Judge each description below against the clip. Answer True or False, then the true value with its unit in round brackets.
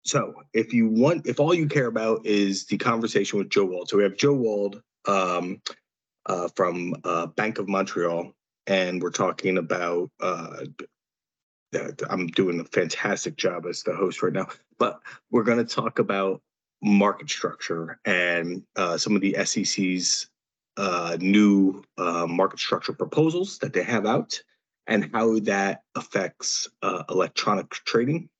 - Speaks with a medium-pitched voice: False (100 Hz)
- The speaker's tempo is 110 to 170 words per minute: True (155 wpm)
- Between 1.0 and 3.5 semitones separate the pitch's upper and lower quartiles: False (4.0 semitones)